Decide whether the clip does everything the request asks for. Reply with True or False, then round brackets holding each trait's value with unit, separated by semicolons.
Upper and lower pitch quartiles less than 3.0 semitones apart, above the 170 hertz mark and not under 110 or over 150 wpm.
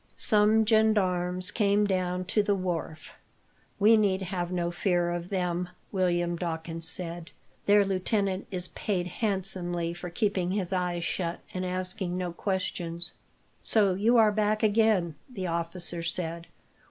True (2.6 semitones; 185 Hz; 140 wpm)